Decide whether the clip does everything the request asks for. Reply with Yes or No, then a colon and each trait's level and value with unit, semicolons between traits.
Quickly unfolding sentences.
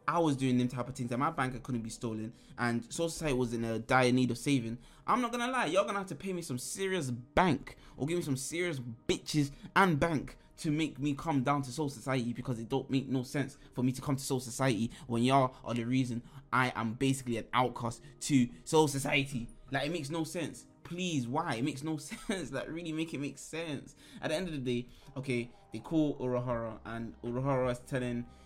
Yes: fast, 230 wpm